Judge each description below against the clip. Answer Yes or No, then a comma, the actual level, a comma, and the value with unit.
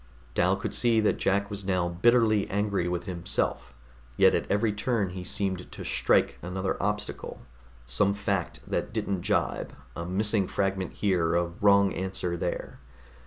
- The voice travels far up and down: No, narrow, 2.4 semitones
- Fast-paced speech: No, average, 155 wpm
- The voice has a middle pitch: No, very low, 95 Hz